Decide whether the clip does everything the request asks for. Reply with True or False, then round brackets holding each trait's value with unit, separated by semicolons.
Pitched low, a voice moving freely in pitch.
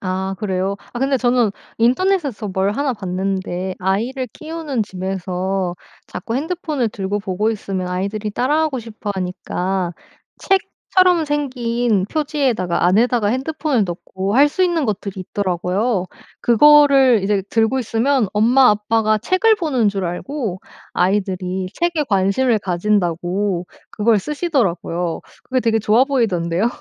False (215 Hz; 5.8 semitones)